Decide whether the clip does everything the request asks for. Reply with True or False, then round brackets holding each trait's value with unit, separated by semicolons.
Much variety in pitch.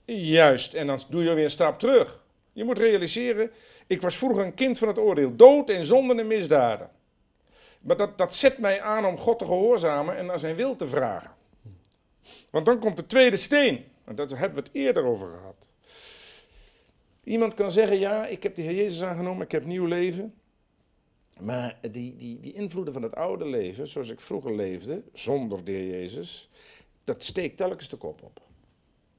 True (6.9 semitones)